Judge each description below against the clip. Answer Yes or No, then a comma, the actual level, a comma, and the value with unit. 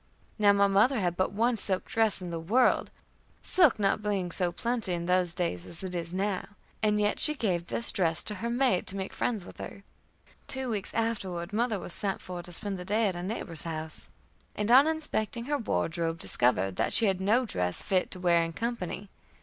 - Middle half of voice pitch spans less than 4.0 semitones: No, average, 4.3 semitones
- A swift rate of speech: Yes, fast, 210 wpm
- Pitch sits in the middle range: No, high, 195 Hz